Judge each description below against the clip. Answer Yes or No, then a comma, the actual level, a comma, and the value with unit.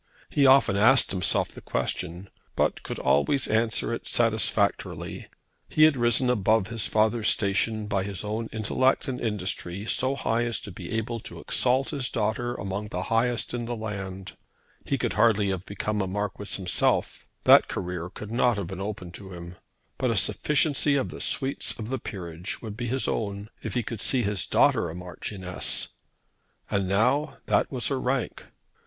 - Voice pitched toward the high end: No, low, 110 Hz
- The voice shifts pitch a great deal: No, average, 3.7 semitones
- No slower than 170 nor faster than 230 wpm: Yes, average, 175 wpm